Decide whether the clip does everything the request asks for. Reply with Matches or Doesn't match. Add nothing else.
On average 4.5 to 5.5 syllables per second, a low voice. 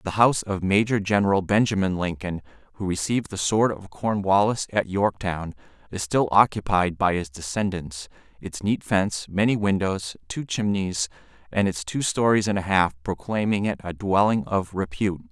Matches